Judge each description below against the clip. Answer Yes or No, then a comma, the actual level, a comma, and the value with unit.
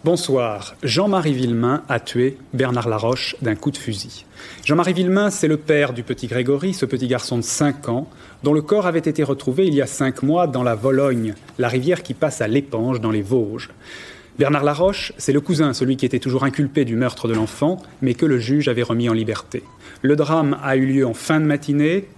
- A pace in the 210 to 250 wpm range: Yes, average, 215 wpm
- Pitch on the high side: No, low, 135 Hz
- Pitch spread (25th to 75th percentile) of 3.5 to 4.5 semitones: Yes, average, 3.8 semitones